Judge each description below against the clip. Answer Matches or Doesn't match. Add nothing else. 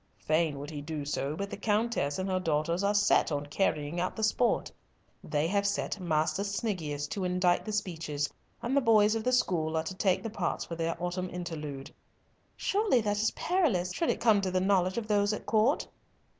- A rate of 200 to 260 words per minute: Matches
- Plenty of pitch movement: Doesn't match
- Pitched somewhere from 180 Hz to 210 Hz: Matches